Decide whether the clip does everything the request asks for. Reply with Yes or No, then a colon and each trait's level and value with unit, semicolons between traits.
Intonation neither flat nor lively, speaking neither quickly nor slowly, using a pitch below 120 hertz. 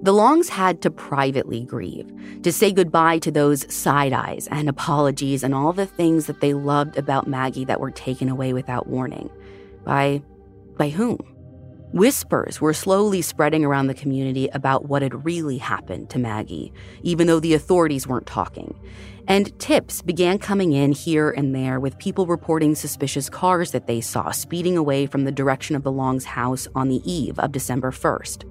No: average, 4.1 semitones; average, 175 wpm; medium, 140 Hz